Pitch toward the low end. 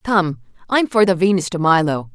No: medium, 180 Hz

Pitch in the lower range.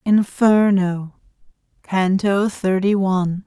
No: high, 195 Hz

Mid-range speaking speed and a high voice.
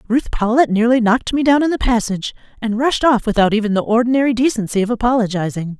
Yes: average, 195 wpm; high, 230 Hz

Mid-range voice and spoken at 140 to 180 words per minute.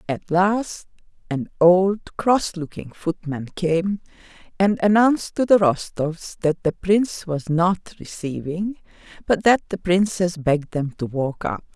Yes: medium, 175 Hz; average, 145 wpm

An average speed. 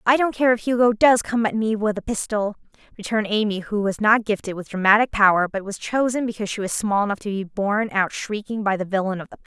No: fast, 255 wpm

